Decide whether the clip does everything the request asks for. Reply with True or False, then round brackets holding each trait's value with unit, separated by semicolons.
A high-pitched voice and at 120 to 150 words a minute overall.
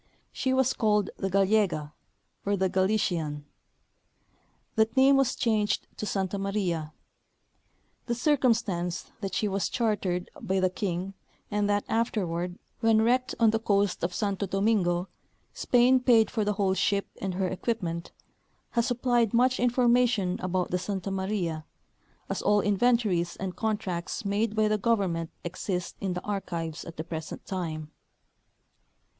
True (200 Hz; 140 wpm)